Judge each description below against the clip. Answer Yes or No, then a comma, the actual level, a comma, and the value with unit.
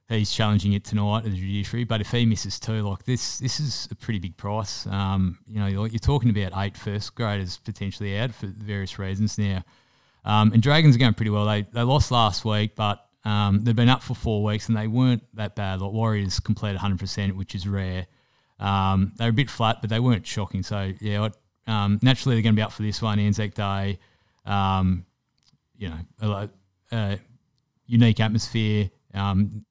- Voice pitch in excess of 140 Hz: No, low, 105 Hz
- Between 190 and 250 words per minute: Yes, fast, 205 wpm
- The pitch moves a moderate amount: No, narrow, 2.3 semitones